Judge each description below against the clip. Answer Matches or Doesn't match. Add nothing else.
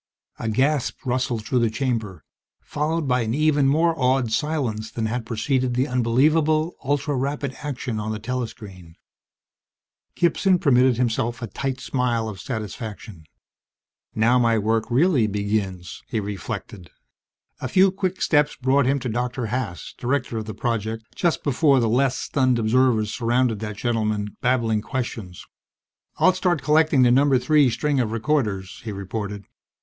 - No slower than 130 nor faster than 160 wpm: Matches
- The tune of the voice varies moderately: Matches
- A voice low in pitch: Matches